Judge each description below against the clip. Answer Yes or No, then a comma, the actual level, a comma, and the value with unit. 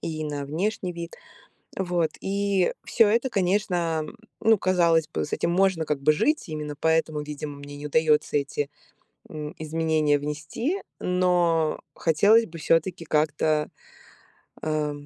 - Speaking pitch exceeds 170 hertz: No, medium, 160 Hz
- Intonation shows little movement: No, average, 3.3 semitones